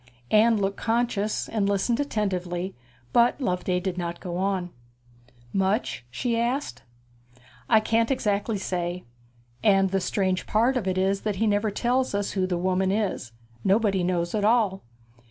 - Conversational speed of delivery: Yes, average, 155 wpm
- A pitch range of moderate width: Yes, average, 3.3 semitones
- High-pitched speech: Yes, high, 200 Hz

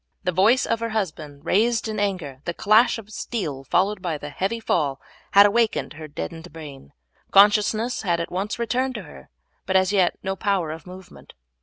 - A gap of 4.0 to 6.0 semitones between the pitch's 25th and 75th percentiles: Yes, average, 5.0 semitones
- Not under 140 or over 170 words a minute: No, average, 185 wpm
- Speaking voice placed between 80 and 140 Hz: No, high, 190 Hz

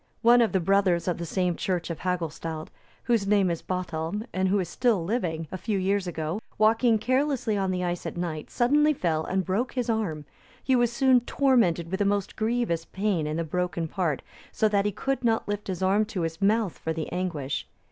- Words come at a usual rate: No, fast, 210 wpm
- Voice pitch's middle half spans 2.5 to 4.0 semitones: No, average, 4.6 semitones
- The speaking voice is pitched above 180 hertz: Yes, high, 190 Hz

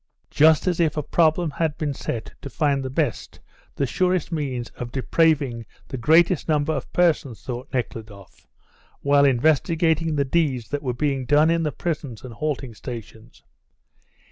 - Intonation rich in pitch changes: No, average, 3.9 semitones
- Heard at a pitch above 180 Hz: No, medium, 145 Hz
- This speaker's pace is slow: No, average, 160 wpm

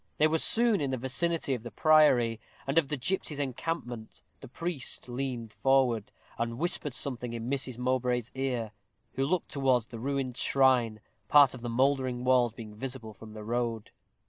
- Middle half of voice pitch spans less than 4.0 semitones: Yes, average, 2.8 semitones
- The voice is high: No, low, 130 Hz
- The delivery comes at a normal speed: Yes, average, 170 wpm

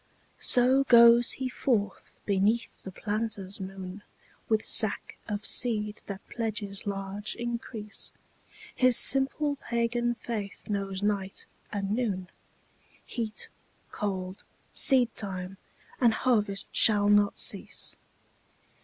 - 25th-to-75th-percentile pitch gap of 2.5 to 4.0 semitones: Yes, average, 3.1 semitones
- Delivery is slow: Yes, slow, 100 wpm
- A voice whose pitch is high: Yes, high, 210 Hz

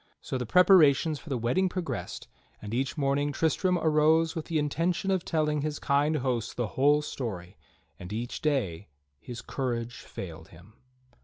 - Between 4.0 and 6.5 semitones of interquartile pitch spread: Yes, average, 4.8 semitones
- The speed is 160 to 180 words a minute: Yes, average, 165 wpm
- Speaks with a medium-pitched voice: Yes, medium, 145 Hz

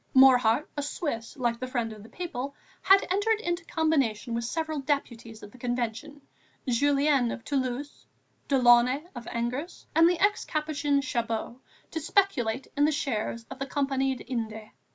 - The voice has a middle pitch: No, very high, 265 Hz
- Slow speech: No, average, 165 wpm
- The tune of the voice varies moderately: Yes, average, 4.2 semitones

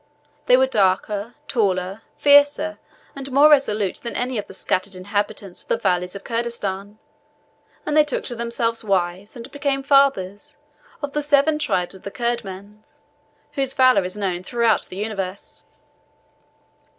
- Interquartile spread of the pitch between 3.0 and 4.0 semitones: No, wide, 5.6 semitones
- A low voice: No, high, 225 Hz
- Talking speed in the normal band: Yes, average, 150 wpm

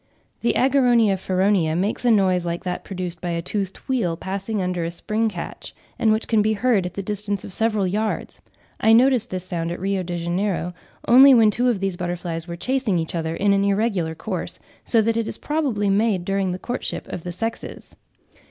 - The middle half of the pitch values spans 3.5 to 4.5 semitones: Yes, average, 4.0 semitones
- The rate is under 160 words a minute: No, fast, 205 wpm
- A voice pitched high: Yes, high, 195 Hz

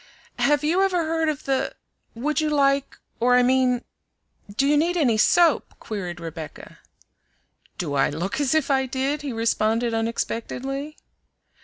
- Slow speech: No, average, 150 wpm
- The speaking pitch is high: Yes, very high, 265 Hz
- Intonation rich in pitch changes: No, average, 4.7 semitones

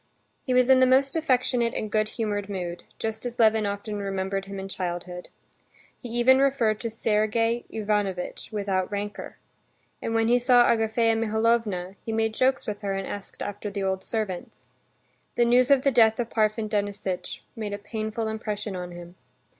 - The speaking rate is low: No, average, 170 wpm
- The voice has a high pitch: Yes, high, 215 Hz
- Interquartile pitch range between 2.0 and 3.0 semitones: Yes, average, 2.7 semitones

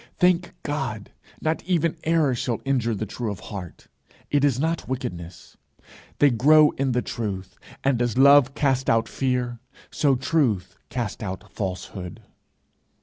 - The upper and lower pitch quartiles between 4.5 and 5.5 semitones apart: Yes, average, 5.2 semitones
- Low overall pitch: Yes, low, 125 Hz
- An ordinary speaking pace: Yes, average, 145 wpm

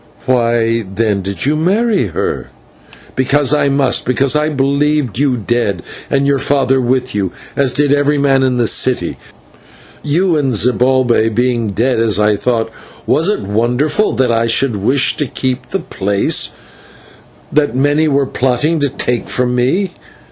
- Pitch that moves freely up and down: No, average, 3.6 semitones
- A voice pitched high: No, low, 130 Hz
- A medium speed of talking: Yes, average, 160 wpm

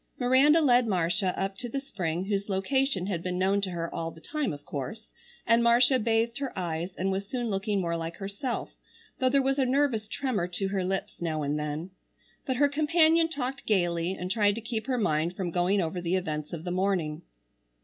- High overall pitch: Yes, high, 195 Hz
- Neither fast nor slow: No, fast, 210 wpm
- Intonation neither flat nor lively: No, wide, 6.2 semitones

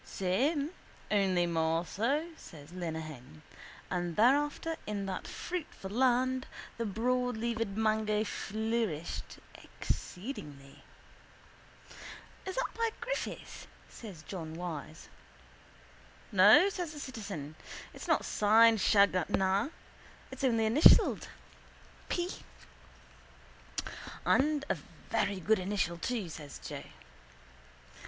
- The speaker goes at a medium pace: No, slow, 95 wpm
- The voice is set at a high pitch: Yes, high, 210 Hz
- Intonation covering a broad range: Yes, wide, 6.1 semitones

